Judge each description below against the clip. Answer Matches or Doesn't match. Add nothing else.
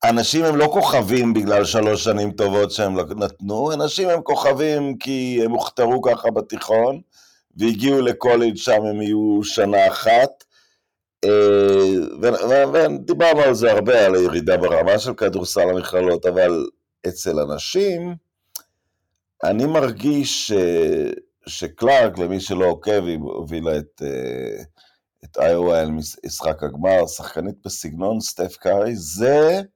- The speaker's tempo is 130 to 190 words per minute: Doesn't match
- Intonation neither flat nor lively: Doesn't match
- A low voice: Matches